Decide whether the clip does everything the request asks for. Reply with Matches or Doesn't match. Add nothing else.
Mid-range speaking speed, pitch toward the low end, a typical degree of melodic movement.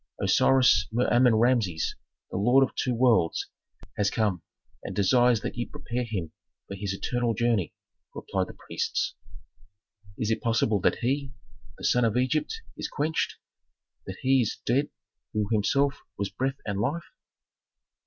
Matches